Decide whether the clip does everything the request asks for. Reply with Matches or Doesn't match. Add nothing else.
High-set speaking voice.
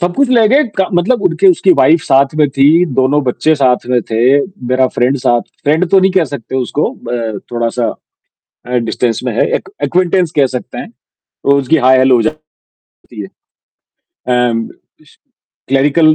Doesn't match